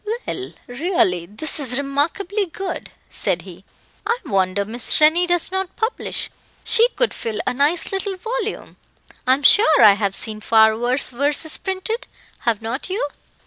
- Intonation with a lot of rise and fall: Yes, wide, 8.9 semitones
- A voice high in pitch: Yes, very high, 295 Hz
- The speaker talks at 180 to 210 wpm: No, average, 155 wpm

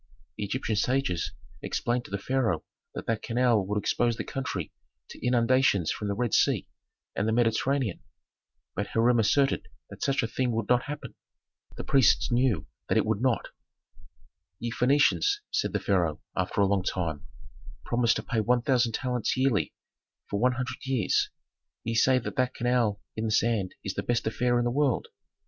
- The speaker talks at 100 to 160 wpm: No, average, 180 wpm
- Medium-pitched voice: No, low, 120 Hz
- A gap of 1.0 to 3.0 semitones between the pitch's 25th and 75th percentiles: No, average, 3.5 semitones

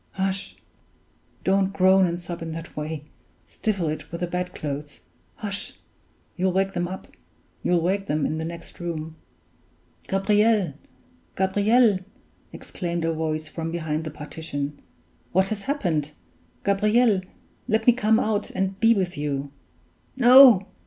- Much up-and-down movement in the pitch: No, average, 3.8 semitones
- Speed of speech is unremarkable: No, slow, 125 wpm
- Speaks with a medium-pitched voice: Yes, medium, 180 Hz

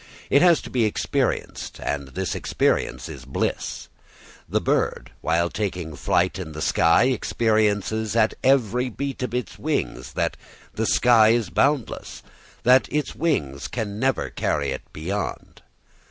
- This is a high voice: No, low, 110 Hz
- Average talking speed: Yes, average, 145 wpm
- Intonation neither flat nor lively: No, wide, 6.6 semitones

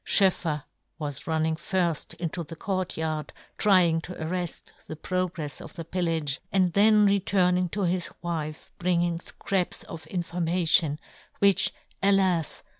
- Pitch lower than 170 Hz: No, medium, 175 Hz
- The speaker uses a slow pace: Yes, slow, 130 wpm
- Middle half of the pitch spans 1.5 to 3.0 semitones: Yes, narrow, 2.5 semitones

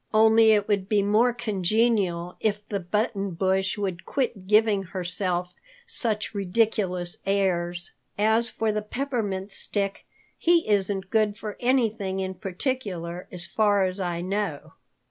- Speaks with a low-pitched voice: No, high, 200 Hz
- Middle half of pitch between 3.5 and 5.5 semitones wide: No, average, 2.8 semitones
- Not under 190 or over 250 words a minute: No, slow, 135 wpm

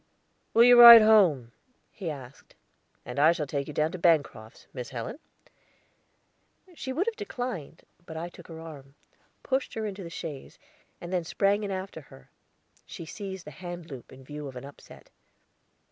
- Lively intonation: Yes, wide, 6.3 semitones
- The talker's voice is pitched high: No, medium, 170 Hz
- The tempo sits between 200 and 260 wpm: No, average, 175 wpm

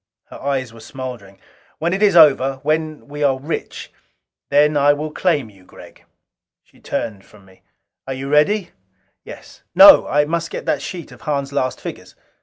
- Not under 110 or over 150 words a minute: No, average, 175 wpm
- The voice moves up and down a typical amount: Yes, average, 3.0 semitones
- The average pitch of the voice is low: No, medium, 145 Hz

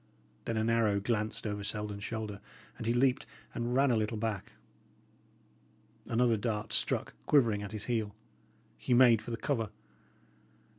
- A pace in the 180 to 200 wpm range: No, average, 150 wpm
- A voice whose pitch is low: Yes, low, 110 Hz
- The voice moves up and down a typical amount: No, narrow, 2.2 semitones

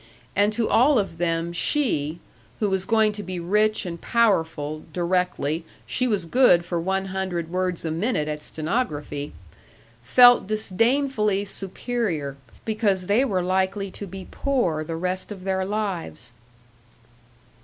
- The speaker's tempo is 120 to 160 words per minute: Yes, average, 140 wpm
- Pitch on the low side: No, high, 190 Hz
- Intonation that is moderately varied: Yes, average, 4.2 semitones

